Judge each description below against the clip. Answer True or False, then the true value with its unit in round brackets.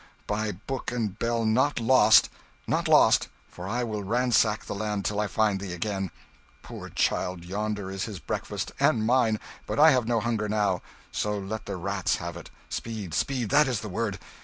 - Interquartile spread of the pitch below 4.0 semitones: True (2.9 semitones)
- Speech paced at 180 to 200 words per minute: True (185 wpm)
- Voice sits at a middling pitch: False (105 Hz)